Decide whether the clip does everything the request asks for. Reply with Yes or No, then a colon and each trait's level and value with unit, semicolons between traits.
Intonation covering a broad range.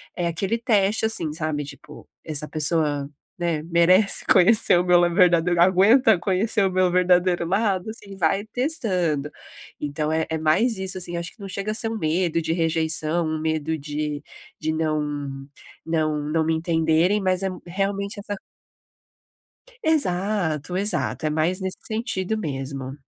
No: average, 3.8 semitones